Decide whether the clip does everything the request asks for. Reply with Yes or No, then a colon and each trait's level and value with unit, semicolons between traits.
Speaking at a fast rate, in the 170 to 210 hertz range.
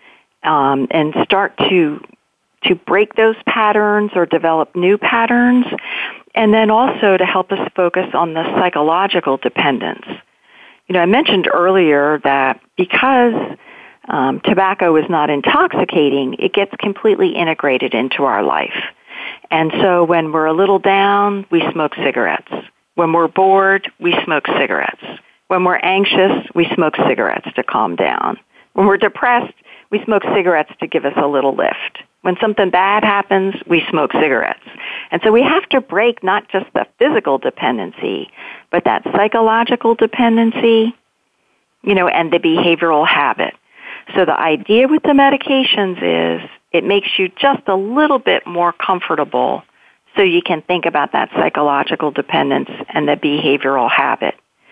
No: average, 150 wpm; high, 190 Hz